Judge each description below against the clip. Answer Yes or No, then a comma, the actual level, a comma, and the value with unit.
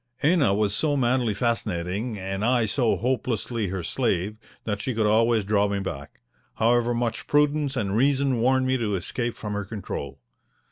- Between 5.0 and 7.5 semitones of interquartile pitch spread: No, average, 3.9 semitones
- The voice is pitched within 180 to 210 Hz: No, low, 115 Hz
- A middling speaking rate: Yes, average, 170 wpm